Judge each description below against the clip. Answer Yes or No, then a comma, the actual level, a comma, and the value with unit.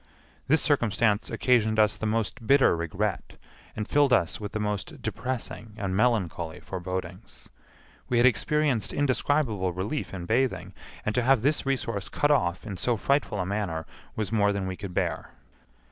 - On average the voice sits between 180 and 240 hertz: No, low, 110 Hz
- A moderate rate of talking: Yes, average, 160 wpm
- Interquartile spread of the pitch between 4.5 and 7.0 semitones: Yes, average, 4.9 semitones